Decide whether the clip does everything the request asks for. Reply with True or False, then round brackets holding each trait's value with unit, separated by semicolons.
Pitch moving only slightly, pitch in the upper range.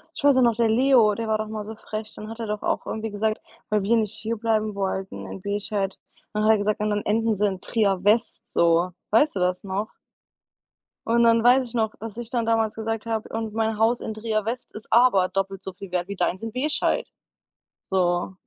True (2.1 semitones; 215 Hz)